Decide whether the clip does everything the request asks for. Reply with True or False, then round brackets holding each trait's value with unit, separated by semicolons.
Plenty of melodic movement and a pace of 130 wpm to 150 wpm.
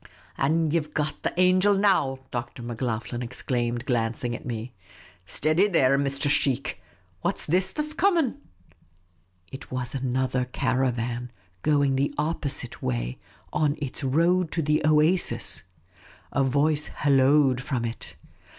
False (3.9 semitones; 145 wpm)